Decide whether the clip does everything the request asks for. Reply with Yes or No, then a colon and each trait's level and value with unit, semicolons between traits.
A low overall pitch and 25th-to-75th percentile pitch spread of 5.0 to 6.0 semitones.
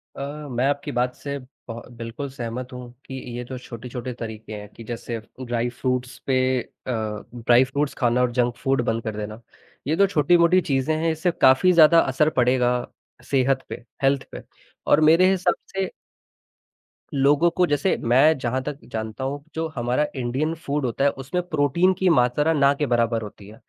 No: low, 130 Hz; average, 3.6 semitones